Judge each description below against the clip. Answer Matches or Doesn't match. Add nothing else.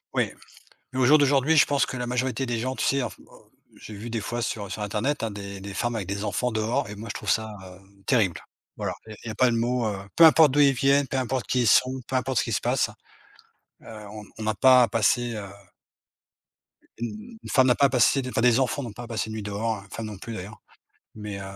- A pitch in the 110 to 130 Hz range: Matches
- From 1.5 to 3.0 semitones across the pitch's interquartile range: Doesn't match